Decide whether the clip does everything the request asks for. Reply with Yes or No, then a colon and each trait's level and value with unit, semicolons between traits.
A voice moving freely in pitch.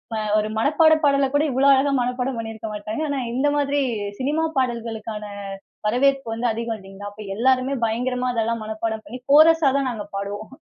No: average, 3.9 semitones